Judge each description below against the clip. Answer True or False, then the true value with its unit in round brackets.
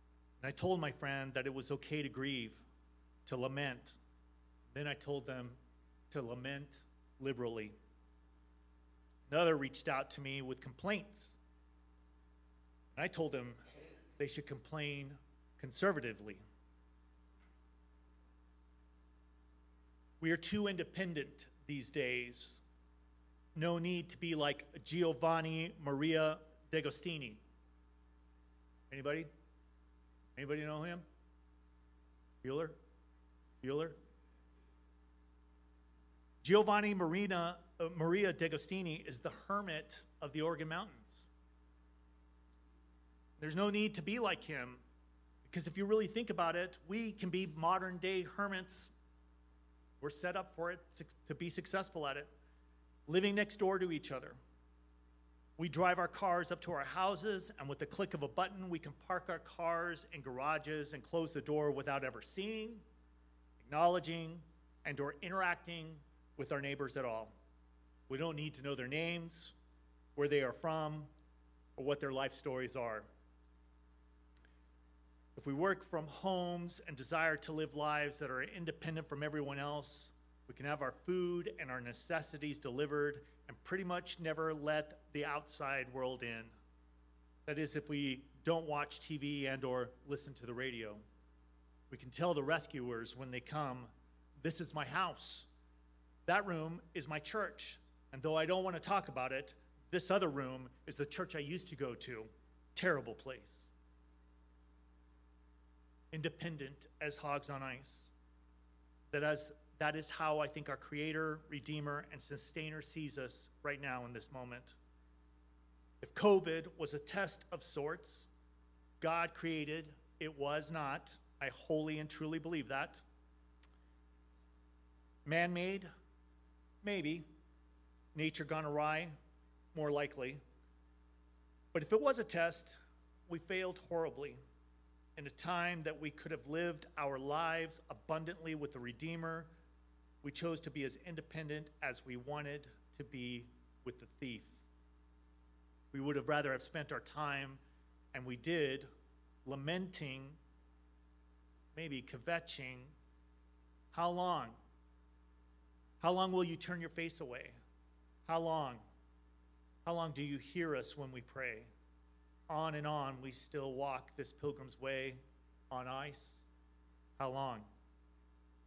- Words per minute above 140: False (135 wpm)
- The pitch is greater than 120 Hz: True (135 Hz)